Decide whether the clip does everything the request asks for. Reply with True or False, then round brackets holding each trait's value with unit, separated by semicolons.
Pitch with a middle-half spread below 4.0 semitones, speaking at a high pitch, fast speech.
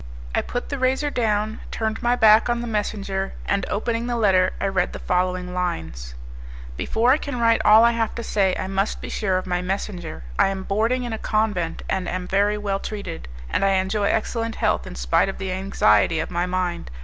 True (3.5 semitones; 200 Hz; 210 wpm)